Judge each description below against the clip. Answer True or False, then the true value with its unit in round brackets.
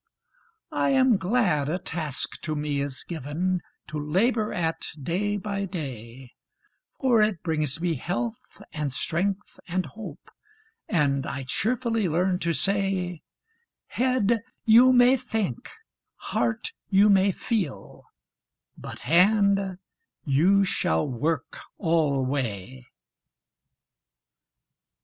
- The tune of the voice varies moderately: False (5.9 semitones)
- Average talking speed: False (105 wpm)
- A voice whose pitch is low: False (180 Hz)